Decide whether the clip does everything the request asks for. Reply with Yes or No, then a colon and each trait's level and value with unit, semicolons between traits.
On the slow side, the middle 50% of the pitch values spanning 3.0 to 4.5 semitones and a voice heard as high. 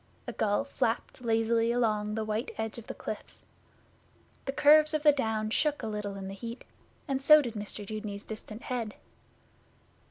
No: average, 170 wpm; average, 3.6 semitones; high, 225 Hz